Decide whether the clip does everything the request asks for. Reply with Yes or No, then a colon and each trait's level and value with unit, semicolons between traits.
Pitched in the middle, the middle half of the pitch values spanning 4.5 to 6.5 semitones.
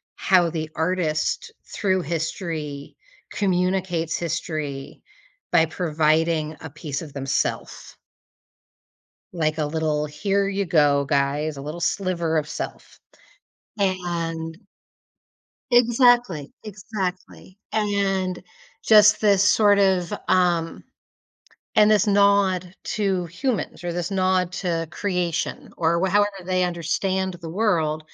No: medium, 175 Hz; average, 3.5 semitones